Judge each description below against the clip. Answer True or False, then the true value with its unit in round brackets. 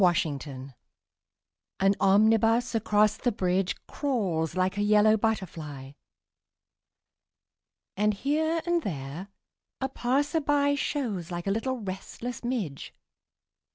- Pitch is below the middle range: False (210 Hz)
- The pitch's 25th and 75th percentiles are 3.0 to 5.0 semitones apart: False (5.4 semitones)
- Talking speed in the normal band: False (115 wpm)